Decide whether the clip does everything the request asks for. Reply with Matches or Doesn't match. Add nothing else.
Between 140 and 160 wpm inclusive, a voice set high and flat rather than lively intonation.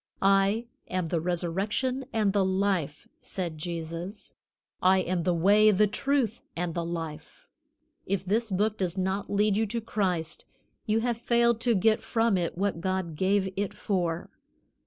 Doesn't match